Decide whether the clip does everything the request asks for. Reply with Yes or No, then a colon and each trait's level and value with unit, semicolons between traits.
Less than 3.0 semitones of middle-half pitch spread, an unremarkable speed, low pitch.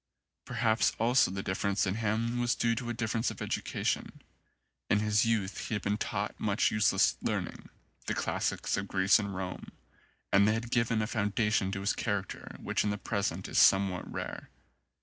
Yes: narrow, 2.4 semitones; average, 190 wpm; low, 105 Hz